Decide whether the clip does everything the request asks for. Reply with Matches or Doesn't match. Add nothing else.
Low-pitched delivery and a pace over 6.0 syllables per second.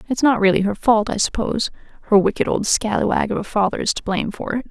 Doesn't match